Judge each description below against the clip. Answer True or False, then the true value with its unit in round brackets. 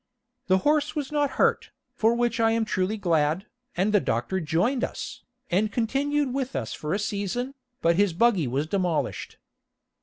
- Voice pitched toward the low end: False (210 Hz)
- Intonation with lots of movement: True (5.8 semitones)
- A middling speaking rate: True (170 wpm)